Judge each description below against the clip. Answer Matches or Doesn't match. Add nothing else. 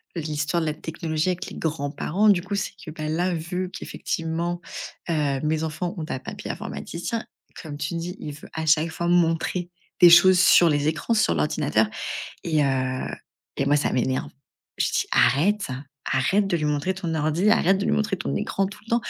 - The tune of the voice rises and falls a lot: Doesn't match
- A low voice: Doesn't match